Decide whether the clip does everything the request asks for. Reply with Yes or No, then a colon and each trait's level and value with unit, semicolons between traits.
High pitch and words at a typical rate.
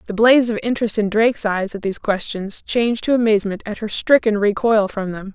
No: high, 215 Hz; fast, 215 wpm